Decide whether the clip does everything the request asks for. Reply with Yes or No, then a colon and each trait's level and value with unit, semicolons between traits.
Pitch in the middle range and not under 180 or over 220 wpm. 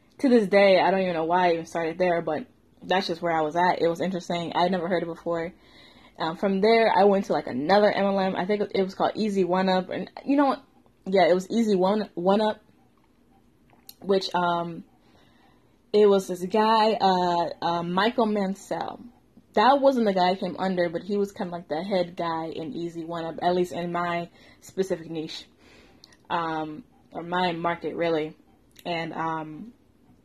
Yes: medium, 180 Hz; average, 195 wpm